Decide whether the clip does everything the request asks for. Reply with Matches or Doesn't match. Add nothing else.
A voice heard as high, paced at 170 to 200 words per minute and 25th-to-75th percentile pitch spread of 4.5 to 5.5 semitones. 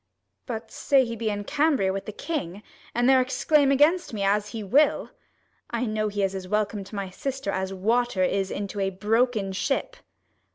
Matches